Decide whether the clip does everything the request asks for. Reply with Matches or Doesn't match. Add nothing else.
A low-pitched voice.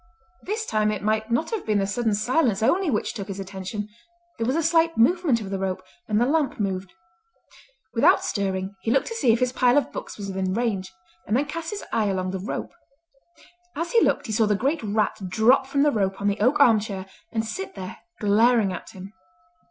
Doesn't match